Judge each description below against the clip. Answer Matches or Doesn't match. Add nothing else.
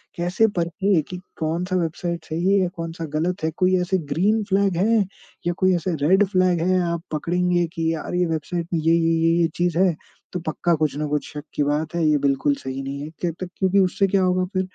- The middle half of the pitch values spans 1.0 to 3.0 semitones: Matches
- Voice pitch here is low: Doesn't match